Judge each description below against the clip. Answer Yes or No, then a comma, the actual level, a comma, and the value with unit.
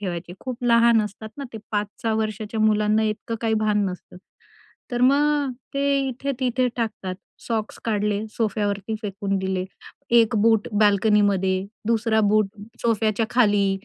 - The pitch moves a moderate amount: No, narrow, 2.3 semitones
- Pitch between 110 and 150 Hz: No, high, 215 Hz